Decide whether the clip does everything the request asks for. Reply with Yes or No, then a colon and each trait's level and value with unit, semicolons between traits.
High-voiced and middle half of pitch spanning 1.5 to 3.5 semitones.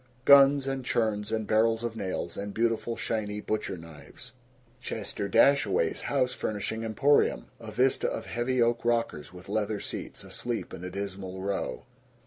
No: low, 110 Hz; average, 3.0 semitones